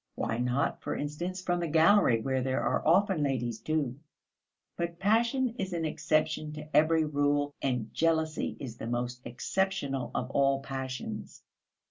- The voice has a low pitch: No, medium, 145 Hz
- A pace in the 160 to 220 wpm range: No, average, 150 wpm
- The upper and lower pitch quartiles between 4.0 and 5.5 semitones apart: Yes, average, 4.6 semitones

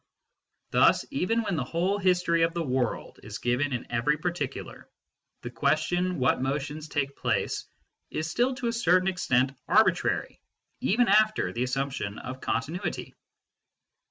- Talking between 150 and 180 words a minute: No, average, 140 wpm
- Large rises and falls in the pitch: Yes, wide, 5.8 semitones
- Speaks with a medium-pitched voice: Yes, medium, 155 Hz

